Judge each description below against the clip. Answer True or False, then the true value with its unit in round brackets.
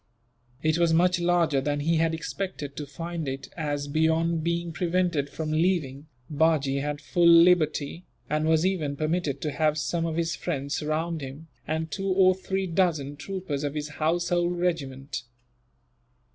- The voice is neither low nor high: True (160 Hz)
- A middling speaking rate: True (160 wpm)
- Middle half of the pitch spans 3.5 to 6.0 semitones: False (2.8 semitones)